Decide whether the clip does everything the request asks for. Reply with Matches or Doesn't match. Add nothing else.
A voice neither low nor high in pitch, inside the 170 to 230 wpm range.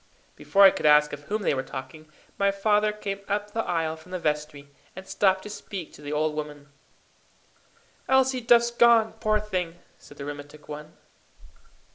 Matches